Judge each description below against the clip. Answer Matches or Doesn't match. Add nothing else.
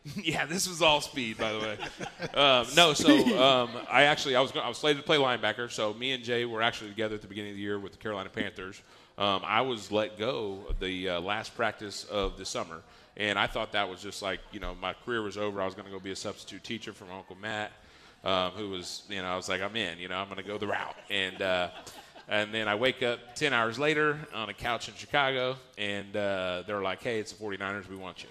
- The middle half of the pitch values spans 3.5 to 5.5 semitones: Matches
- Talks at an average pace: Doesn't match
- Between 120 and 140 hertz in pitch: Doesn't match